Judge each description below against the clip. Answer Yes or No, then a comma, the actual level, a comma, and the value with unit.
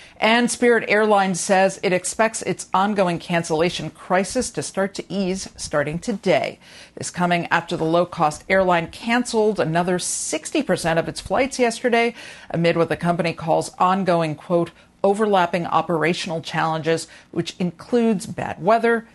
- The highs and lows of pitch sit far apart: No, average, 4.3 semitones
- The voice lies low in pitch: No, medium, 185 Hz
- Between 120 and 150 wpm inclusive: Yes, slow, 135 wpm